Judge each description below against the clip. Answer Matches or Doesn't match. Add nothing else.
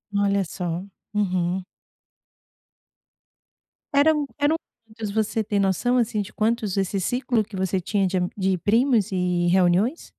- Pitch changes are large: Doesn't match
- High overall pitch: Matches